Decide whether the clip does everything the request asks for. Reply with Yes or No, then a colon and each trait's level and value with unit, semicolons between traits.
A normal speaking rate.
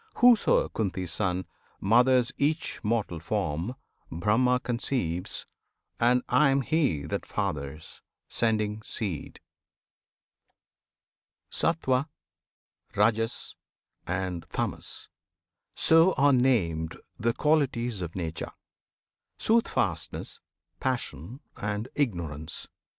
No: slow, 85 wpm